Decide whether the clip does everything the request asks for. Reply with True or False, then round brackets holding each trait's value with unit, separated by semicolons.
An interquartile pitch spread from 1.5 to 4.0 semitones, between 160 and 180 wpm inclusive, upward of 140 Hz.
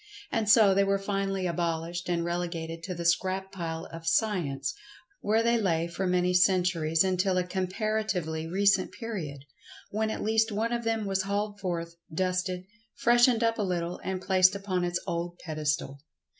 True (3.1 semitones; 170 wpm; 185 Hz)